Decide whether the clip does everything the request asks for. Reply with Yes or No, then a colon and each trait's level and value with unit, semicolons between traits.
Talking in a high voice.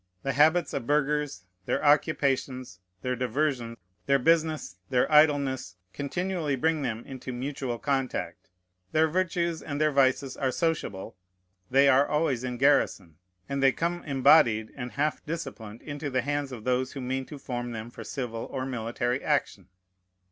No: low, 135 Hz